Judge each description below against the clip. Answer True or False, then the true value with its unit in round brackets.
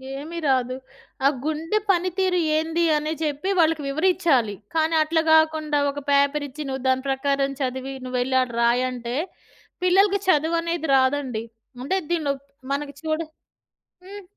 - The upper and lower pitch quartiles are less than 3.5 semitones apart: False (3.8 semitones)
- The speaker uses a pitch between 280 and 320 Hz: True (300 Hz)